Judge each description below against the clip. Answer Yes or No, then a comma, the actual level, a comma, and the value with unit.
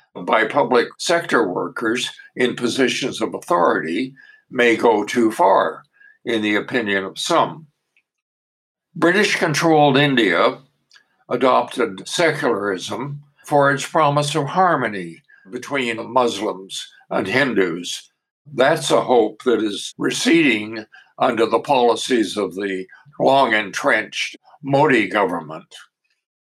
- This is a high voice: No, low, 135 Hz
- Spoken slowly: Yes, slow, 105 wpm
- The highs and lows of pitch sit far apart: Yes, wide, 7.1 semitones